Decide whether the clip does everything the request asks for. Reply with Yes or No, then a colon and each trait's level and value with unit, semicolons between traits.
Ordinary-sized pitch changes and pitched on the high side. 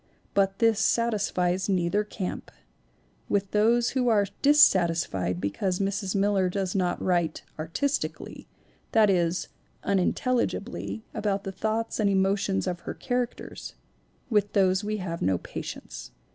Yes: average, 3.0 semitones; high, 195 Hz